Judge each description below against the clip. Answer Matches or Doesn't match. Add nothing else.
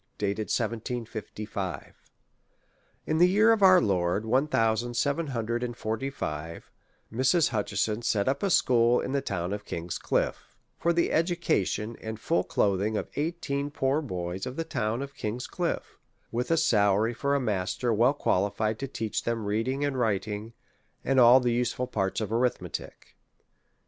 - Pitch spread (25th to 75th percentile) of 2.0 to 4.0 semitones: Doesn't match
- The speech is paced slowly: Doesn't match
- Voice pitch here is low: Matches